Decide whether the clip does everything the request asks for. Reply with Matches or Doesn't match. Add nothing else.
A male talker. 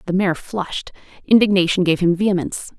Doesn't match